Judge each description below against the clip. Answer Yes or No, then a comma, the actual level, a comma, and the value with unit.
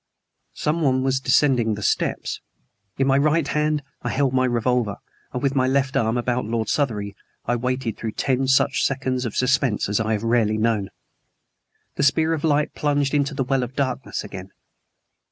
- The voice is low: Yes, low, 130 Hz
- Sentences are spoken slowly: No, average, 175 wpm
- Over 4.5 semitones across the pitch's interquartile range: No, average, 3.2 semitones